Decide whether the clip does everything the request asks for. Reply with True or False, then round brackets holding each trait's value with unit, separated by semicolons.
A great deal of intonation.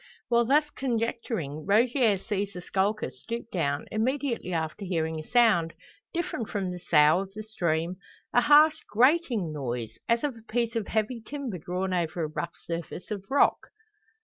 True (5.7 semitones)